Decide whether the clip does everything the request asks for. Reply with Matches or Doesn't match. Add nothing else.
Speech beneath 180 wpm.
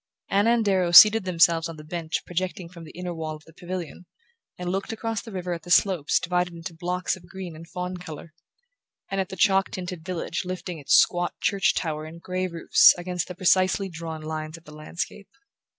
Doesn't match